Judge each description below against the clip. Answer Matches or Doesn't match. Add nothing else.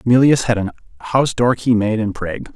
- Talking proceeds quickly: Matches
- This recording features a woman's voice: Doesn't match